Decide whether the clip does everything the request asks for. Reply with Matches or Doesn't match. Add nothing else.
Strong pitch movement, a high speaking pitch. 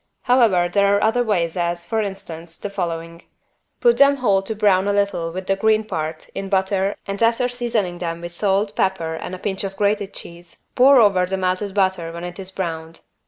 Doesn't match